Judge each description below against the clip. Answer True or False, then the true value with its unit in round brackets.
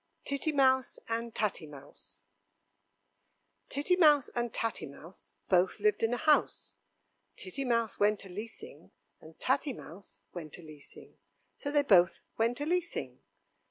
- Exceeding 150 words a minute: False (140 wpm)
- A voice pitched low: False (230 Hz)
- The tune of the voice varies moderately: False (7.2 semitones)